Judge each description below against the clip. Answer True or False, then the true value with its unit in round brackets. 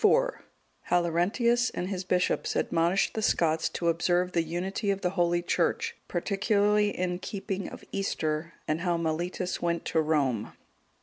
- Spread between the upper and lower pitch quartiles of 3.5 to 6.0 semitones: False (2.7 semitones)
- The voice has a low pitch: False (180 Hz)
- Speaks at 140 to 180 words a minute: True (145 wpm)